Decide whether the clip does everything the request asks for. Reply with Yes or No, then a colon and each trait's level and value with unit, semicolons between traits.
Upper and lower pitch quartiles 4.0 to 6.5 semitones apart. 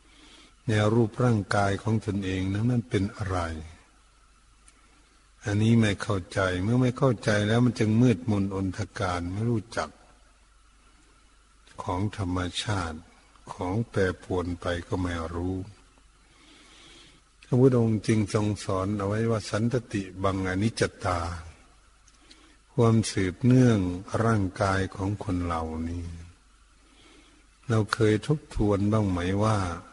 No: average, 3.5 semitones